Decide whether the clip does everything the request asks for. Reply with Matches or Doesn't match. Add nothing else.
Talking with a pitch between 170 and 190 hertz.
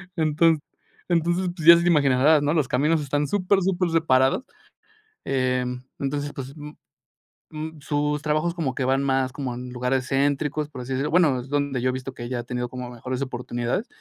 Doesn't match